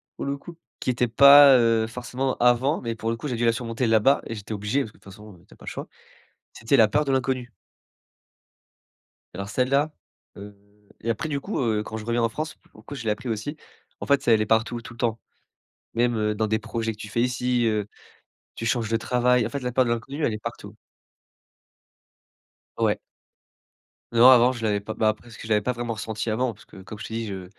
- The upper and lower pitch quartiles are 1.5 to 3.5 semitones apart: Yes, narrow, 2.5 semitones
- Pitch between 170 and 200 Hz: No, low, 115 Hz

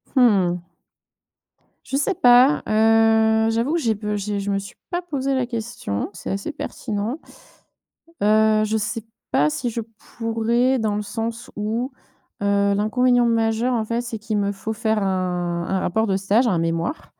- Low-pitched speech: No, high, 220 Hz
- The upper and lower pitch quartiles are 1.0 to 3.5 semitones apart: Yes, average, 2.8 semitones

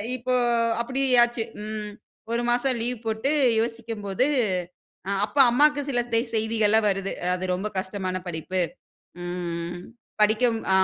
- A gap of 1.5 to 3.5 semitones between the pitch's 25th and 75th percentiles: No, average, 4.1 semitones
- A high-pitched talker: Yes, high, 220 Hz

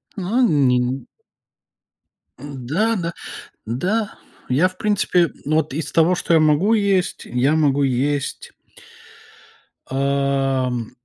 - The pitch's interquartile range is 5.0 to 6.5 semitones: Yes, average, 5.3 semitones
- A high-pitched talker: No, medium, 145 Hz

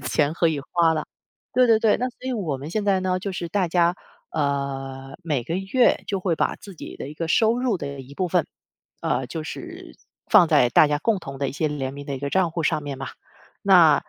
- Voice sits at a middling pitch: Yes, medium, 160 Hz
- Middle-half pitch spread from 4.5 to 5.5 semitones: Yes, average, 5.2 semitones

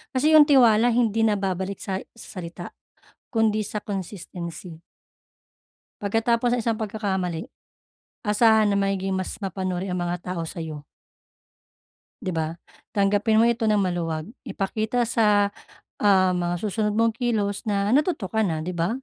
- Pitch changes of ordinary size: Yes, average, 3.4 semitones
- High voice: Yes, high, 200 Hz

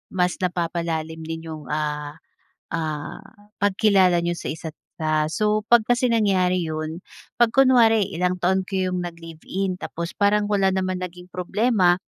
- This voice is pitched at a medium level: Yes, medium, 180 Hz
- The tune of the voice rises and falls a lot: No, average, 3.7 semitones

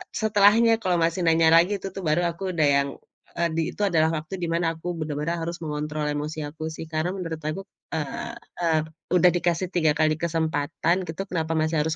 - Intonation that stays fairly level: Yes, narrow, 2.2 semitones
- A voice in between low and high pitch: Yes, medium, 165 Hz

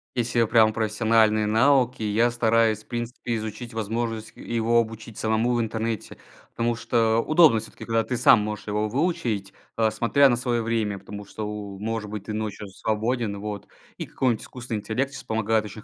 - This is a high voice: No, low, 110 Hz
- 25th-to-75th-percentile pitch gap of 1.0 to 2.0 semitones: Yes, narrow, 1.6 semitones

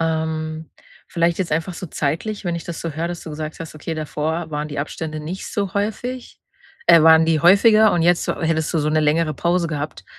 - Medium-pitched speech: Yes, medium, 160 Hz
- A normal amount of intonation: No, narrow, 2.0 semitones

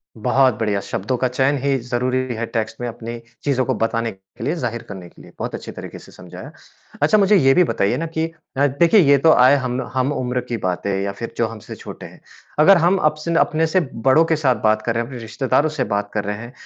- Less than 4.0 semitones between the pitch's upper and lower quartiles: No, average, 4.7 semitones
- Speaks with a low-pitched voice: Yes, low, 125 Hz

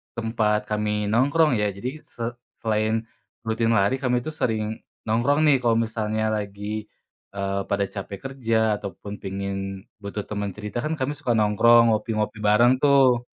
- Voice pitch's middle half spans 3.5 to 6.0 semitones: No, narrow, 2.5 semitones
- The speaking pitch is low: Yes, low, 110 Hz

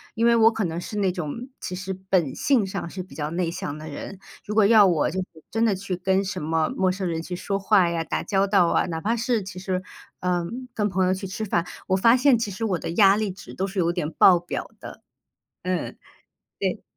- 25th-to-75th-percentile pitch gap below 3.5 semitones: Yes, average, 2.7 semitones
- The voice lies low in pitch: No, high, 190 Hz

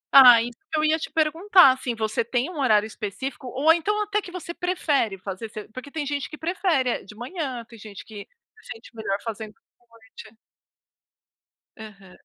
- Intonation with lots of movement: Yes, wide, 6.4 semitones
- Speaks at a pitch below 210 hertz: No, very high, 255 Hz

